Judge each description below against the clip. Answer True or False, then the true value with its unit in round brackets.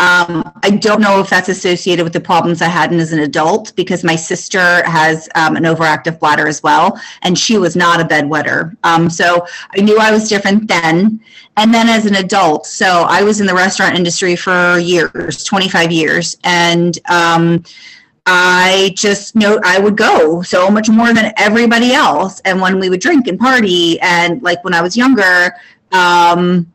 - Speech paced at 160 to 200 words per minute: True (190 wpm)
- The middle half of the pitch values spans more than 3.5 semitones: False (3.1 semitones)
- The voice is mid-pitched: True (180 Hz)